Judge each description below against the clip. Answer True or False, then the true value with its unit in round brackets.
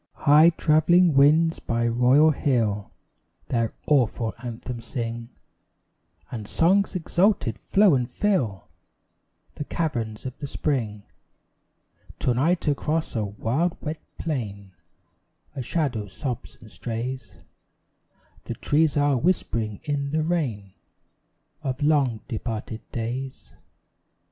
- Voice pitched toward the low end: True (130 Hz)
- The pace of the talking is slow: True (110 wpm)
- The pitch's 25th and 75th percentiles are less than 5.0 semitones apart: False (5.3 semitones)